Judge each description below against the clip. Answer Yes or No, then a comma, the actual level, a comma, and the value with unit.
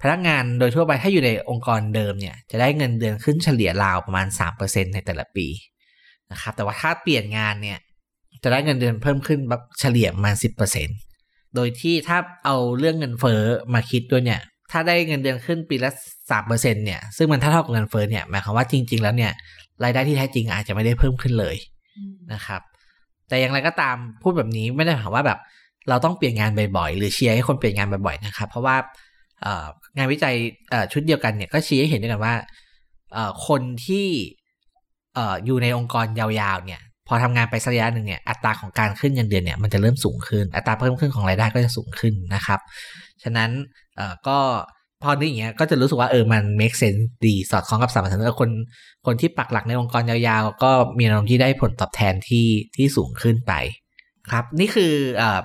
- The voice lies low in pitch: Yes, low, 120 Hz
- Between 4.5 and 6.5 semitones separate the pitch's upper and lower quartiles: No, average, 4.0 semitones